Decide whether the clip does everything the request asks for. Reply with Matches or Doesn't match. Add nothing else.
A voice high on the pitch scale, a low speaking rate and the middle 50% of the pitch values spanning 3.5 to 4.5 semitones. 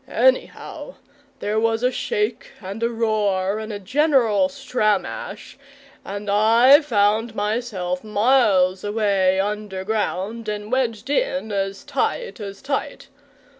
Matches